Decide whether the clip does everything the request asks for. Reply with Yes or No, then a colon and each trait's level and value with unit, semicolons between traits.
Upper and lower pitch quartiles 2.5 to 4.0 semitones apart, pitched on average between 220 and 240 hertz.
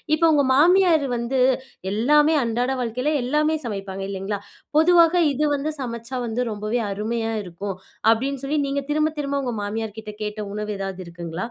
No: wide, 5.6 semitones; high, 235 Hz